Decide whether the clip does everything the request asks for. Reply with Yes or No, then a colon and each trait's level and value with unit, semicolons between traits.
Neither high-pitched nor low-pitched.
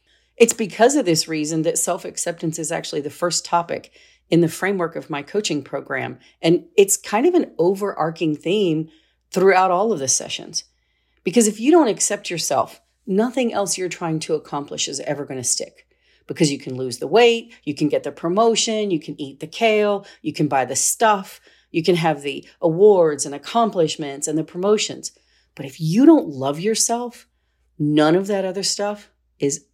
Yes: medium, 175 Hz